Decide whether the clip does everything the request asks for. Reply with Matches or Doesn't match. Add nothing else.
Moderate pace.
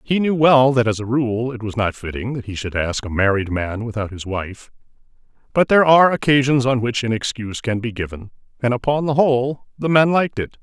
Doesn't match